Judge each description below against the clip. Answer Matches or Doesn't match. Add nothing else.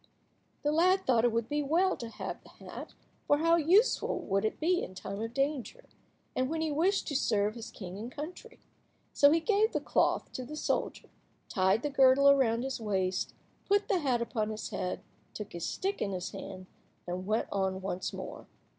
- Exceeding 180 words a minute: Matches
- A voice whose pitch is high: Matches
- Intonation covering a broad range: Matches